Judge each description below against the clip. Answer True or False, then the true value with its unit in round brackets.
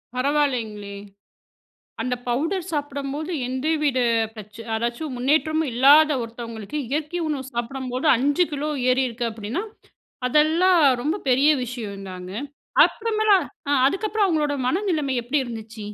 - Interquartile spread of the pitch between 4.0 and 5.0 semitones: True (4.7 semitones)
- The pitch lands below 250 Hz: False (275 Hz)